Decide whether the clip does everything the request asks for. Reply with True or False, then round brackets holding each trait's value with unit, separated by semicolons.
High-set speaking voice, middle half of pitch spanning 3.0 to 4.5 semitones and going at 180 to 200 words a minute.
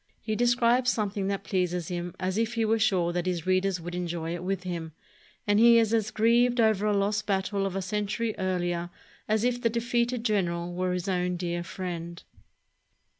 True (195 Hz; 3.9 semitones; 190 wpm)